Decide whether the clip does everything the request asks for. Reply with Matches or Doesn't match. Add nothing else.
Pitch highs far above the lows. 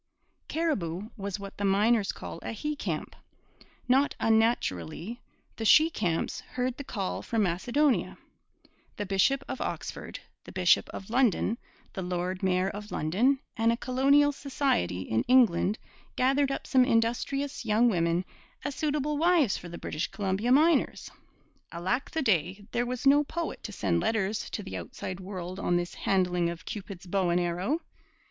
Matches